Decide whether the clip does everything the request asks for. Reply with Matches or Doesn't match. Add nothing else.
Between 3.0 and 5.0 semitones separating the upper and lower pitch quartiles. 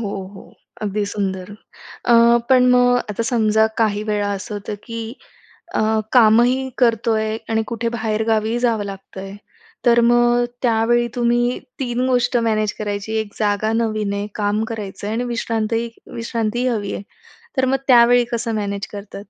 Doesn't match